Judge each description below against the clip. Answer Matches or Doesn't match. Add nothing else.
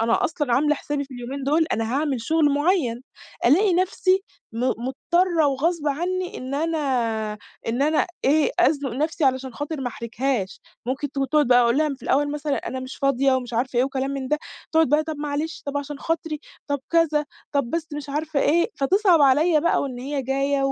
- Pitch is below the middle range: Doesn't match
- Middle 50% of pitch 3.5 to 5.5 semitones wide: Doesn't match